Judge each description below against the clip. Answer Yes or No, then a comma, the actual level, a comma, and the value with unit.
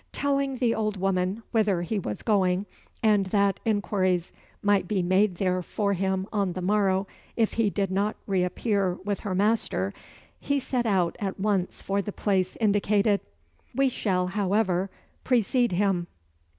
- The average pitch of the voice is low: No, high, 200 Hz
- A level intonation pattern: Yes, narrow, 2.3 semitones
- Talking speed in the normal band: Yes, average, 155 wpm